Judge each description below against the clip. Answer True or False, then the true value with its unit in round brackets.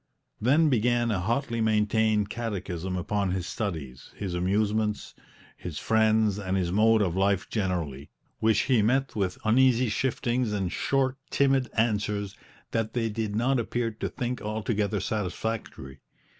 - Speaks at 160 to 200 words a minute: False (140 wpm)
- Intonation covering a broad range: False (3.3 semitones)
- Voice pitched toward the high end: False (110 Hz)